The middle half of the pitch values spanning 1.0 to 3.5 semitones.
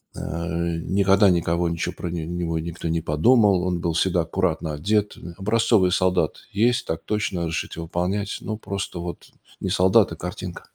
Yes: average, 2.8 semitones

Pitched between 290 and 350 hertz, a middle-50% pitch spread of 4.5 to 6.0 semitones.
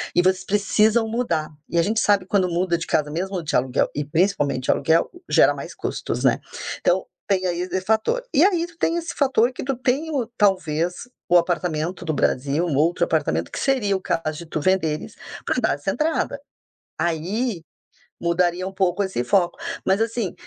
No: medium, 185 Hz; average, 5.0 semitones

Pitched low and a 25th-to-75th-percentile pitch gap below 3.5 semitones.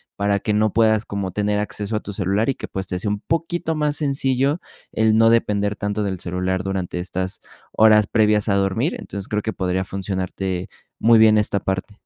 Yes: low, 105 Hz; narrow, 2.5 semitones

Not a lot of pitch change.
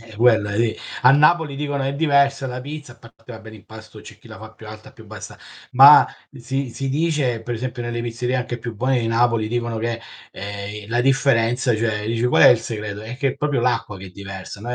No: average, 3.3 semitones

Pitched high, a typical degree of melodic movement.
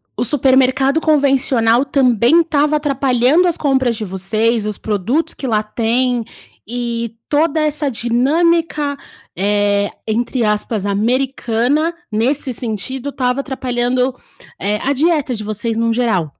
Yes: very high, 250 Hz; average, 3.9 semitones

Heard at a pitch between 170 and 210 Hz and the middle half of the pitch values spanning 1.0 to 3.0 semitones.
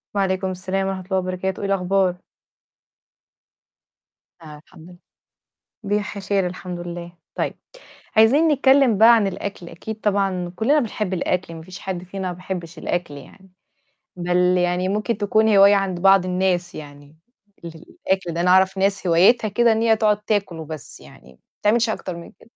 Yes: high, 190 Hz; narrow, 2.6 semitones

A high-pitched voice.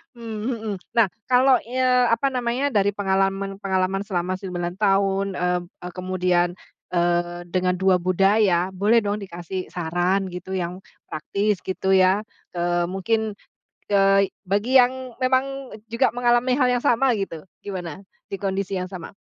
Yes: high, 195 Hz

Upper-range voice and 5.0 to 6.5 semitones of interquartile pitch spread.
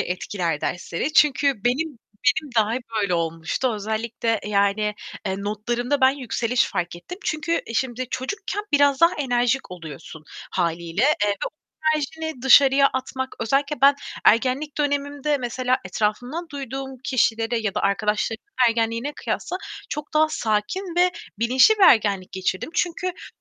Yes: very high, 250 Hz; average, 5.3 semitones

